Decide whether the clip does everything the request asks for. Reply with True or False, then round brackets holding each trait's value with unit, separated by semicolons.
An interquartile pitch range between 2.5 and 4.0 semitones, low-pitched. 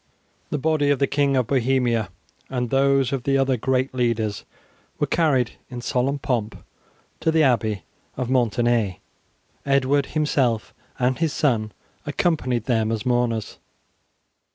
True (2.8 semitones; 130 Hz)